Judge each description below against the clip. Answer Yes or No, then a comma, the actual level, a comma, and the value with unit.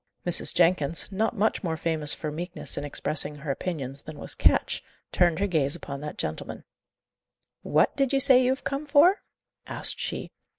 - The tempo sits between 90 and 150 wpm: No, average, 175 wpm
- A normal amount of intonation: No, wide, 7.1 semitones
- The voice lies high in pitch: No, medium, 170 Hz